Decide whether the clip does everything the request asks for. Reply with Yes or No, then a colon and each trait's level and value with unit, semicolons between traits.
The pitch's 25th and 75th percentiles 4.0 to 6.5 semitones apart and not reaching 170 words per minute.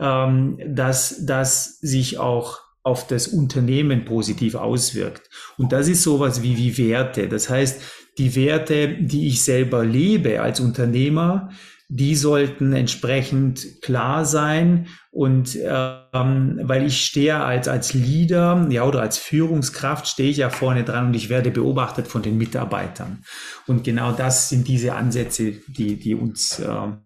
No: narrow, 2.6 semitones; average, 145 wpm